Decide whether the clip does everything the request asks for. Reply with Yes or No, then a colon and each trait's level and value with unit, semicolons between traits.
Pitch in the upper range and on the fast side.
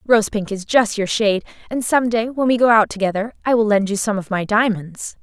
Yes: high, 215 Hz; fast, 255 wpm